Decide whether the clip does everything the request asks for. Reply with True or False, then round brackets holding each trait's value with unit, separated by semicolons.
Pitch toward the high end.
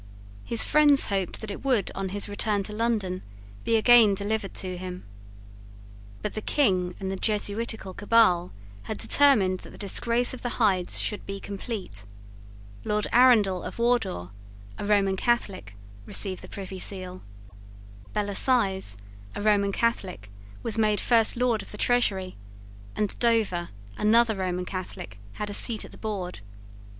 True (205 Hz)